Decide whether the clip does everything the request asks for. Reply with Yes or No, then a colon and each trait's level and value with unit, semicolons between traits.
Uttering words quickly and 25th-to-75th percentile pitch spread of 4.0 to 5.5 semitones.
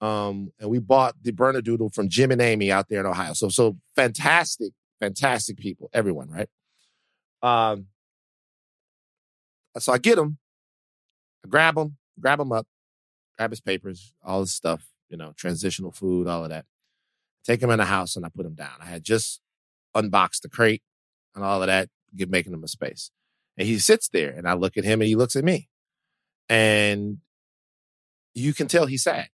No: average, 185 wpm; average, 4.6 semitones